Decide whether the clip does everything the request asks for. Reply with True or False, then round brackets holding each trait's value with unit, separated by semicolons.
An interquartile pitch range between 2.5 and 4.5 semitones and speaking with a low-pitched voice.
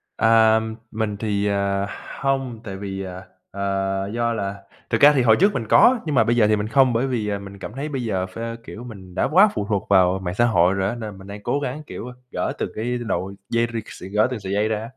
True (3.3 semitones; 110 Hz)